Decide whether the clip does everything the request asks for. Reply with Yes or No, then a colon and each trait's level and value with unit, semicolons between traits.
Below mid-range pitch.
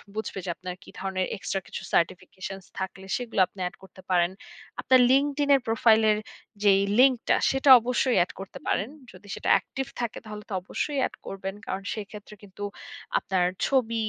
No: high, 205 Hz